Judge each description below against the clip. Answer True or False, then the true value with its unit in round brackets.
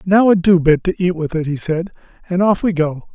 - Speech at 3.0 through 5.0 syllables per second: False (5.4 syllables/s)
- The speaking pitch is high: False (175 Hz)